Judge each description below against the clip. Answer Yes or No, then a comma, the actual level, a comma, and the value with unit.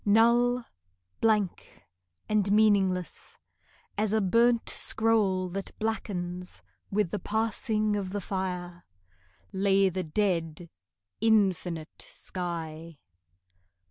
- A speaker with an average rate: No, slow, 90 wpm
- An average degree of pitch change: Yes, average, 3.4 semitones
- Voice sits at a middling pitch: No, high, 195 Hz